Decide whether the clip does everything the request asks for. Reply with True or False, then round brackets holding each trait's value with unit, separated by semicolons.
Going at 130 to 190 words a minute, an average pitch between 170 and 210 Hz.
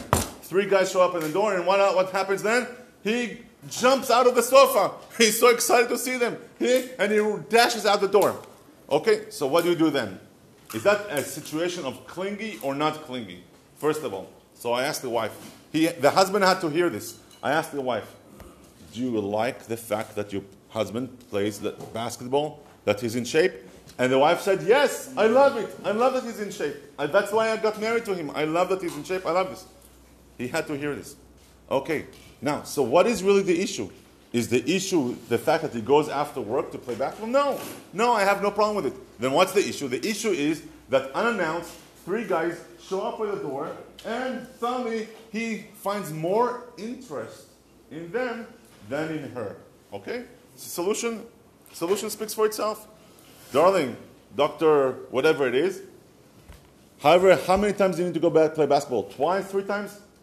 False (200 wpm; 190 Hz)